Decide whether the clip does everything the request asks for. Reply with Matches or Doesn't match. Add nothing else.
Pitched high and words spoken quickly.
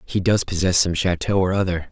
Doesn't match